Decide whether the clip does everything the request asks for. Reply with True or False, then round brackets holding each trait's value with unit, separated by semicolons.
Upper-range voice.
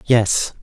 False (125 Hz)